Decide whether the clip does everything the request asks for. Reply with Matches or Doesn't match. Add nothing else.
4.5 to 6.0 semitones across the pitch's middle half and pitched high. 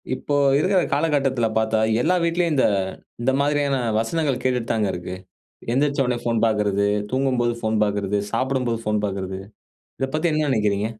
Doesn't match